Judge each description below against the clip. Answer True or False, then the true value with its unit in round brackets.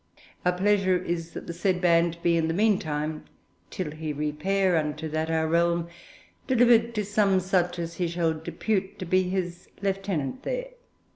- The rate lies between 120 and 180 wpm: True (165 wpm)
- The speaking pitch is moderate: True (175 Hz)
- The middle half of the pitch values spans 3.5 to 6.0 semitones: False (3.0 semitones)